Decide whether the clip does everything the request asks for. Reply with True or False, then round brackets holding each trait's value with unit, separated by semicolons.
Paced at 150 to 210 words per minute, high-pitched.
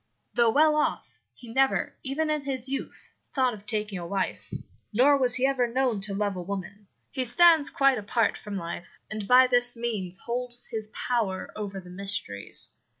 True (180 wpm; 235 Hz)